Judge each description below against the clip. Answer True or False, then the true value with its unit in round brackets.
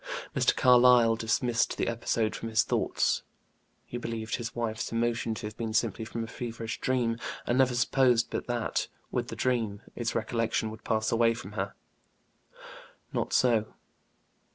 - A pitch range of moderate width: False (1.4 semitones)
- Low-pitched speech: True (115 Hz)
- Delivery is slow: False (155 wpm)